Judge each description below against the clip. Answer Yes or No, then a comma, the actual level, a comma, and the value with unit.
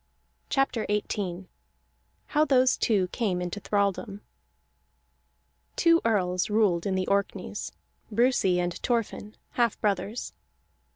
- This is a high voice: Yes, high, 205 Hz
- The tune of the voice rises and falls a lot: No, average, 3.9 semitones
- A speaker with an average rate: No, slow, 105 wpm